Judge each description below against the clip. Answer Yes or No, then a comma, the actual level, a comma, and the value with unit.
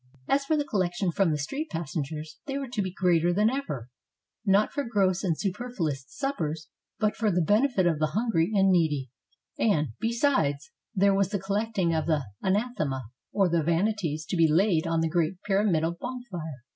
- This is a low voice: No, medium, 185 Hz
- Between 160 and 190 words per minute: Yes, average, 185 wpm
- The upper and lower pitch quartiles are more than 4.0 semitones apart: Yes, average, 5.1 semitones